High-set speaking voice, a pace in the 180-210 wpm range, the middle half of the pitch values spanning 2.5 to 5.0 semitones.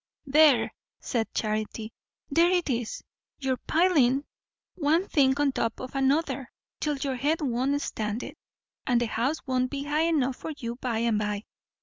No: very high, 265 Hz; average, 160 wpm; average, 3.8 semitones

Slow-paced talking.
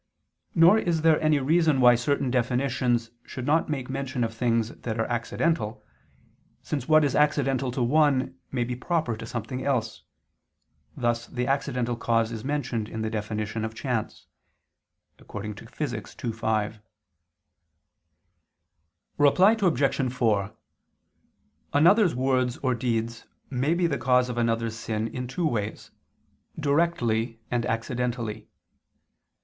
Yes: slow, 130 wpm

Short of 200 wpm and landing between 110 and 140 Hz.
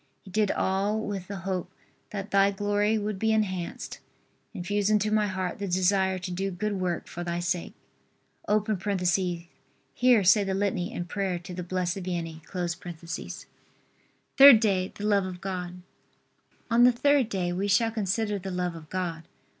No: average, 160 wpm; high, 190 Hz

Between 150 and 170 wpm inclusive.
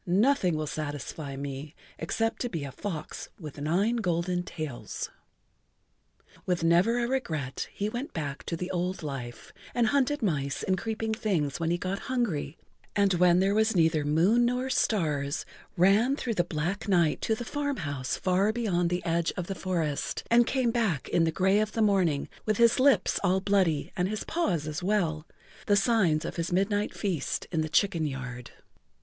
No: average, 180 wpm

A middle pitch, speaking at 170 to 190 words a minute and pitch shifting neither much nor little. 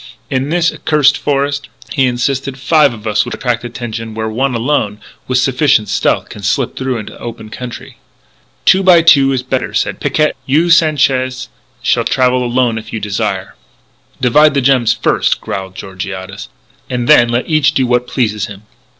No: low, 125 Hz; average, 175 wpm; average, 3.7 semitones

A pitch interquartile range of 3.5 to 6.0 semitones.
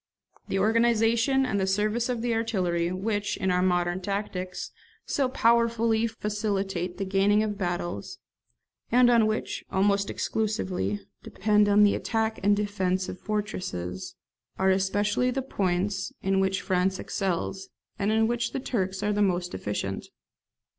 No: average, 2.9 semitones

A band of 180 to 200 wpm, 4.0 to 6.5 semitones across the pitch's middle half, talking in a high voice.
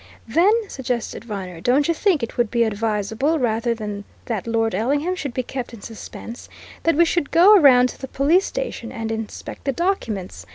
Yes: average, 190 wpm; average, 5.0 semitones; high, 245 Hz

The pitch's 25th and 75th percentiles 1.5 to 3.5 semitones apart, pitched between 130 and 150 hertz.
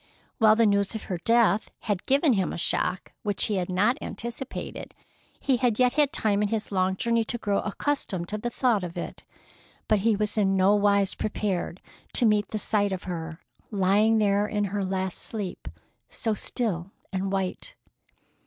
No: average, 2.8 semitones; high, 205 Hz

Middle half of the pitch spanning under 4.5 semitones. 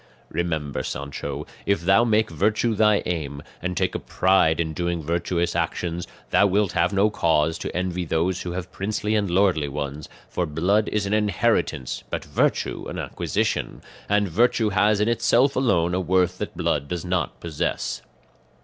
Yes: average, 3.8 semitones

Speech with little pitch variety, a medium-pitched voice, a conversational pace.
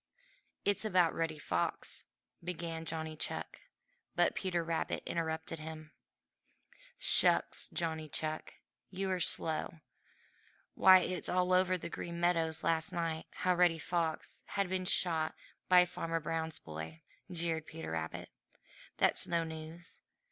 No: narrow, 2.0 semitones; medium, 165 Hz; slow, 125 wpm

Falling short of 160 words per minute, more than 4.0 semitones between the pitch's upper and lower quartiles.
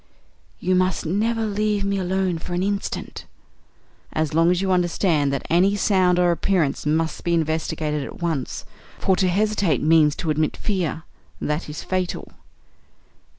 No: average, 150 wpm; average, 3.3 semitones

